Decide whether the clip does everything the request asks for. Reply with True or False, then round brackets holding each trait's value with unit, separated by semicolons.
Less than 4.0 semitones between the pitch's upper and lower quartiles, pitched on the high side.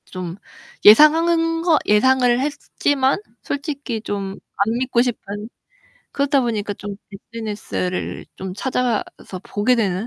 False (5.3 semitones; 240 Hz)